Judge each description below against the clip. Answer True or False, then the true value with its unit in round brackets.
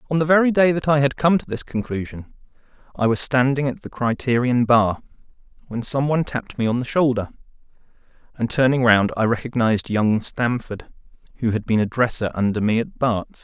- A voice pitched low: True (125 Hz)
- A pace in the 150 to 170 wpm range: False (190 wpm)